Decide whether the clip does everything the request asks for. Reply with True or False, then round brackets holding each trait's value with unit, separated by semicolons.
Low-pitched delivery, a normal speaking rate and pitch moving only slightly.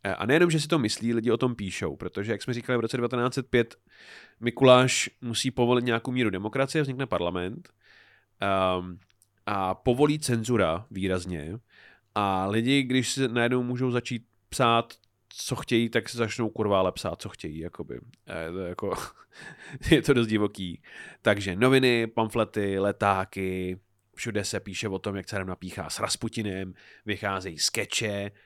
False (110 Hz; 150 wpm; 4.2 semitones)